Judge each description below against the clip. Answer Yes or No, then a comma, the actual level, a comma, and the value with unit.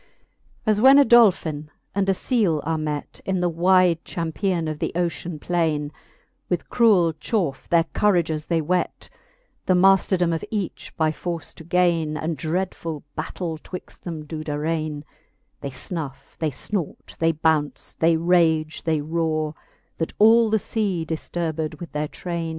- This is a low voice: No, medium, 165 Hz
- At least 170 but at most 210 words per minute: No, average, 150 wpm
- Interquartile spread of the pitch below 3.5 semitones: Yes, average, 2.7 semitones